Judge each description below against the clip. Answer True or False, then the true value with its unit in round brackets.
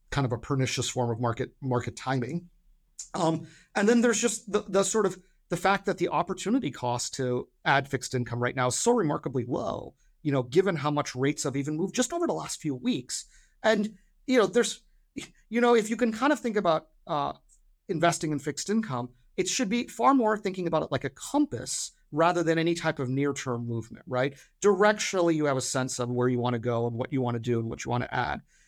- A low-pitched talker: False (160 Hz)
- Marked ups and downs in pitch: True (8.0 semitones)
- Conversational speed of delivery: False (230 wpm)